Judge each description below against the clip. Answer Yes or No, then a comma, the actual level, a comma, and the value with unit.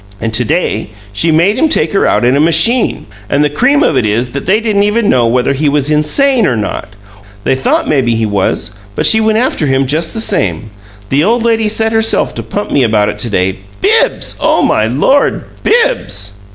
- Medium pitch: Yes, medium, 150 Hz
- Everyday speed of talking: No, fast, 215 wpm